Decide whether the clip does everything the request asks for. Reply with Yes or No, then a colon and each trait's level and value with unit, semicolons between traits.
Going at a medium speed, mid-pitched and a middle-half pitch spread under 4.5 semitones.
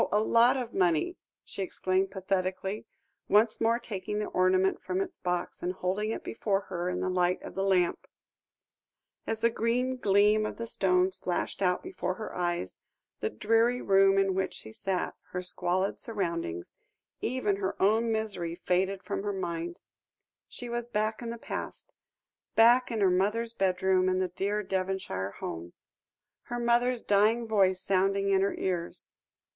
No: average, 160 wpm; high, 195 Hz; average, 3.2 semitones